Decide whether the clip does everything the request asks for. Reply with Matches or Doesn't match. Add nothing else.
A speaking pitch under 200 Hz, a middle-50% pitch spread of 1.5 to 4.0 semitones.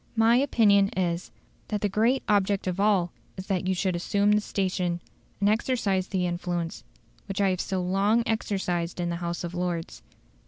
Matches